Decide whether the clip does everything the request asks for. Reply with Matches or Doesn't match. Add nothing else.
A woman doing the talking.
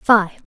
Matches